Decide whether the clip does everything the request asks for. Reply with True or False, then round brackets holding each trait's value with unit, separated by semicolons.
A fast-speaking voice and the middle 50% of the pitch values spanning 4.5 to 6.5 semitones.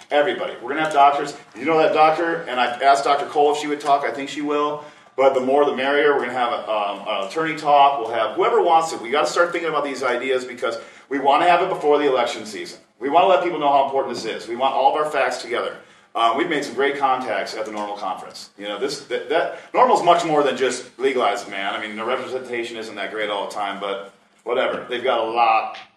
False (260 wpm; 3.7 semitones)